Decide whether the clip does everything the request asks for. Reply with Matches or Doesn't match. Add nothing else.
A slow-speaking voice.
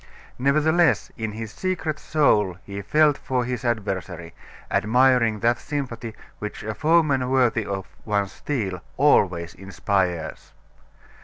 Matches